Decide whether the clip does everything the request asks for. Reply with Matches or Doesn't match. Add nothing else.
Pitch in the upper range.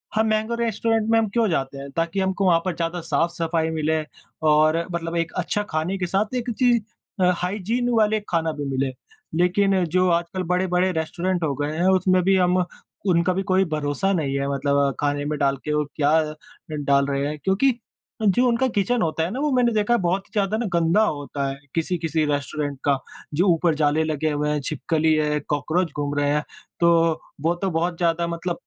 Doesn't match